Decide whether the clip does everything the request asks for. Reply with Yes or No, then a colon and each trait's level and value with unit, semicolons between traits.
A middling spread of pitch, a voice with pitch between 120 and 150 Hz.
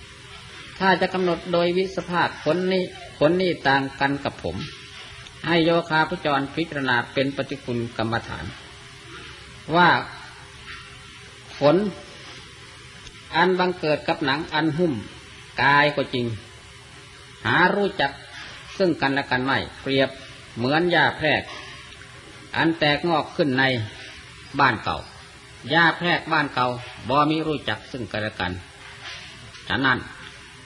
Yes: average, 4.6 semitones; medium, 140 Hz